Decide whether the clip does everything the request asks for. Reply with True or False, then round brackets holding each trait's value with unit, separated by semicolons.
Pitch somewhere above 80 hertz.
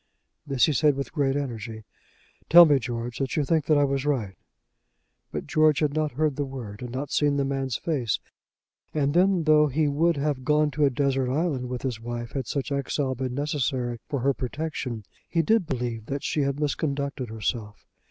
True (140 Hz)